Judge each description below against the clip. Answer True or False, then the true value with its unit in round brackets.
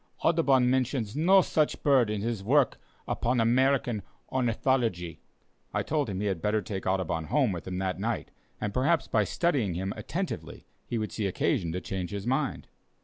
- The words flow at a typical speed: True (175 wpm)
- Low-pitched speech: True (115 Hz)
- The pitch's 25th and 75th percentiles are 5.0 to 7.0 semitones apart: True (5.6 semitones)